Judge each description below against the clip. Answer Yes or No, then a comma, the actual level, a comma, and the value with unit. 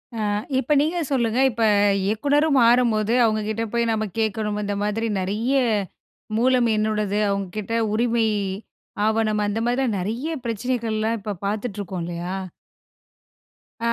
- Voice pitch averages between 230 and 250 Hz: No, high, 220 Hz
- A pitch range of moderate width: No, narrow, 2.3 semitones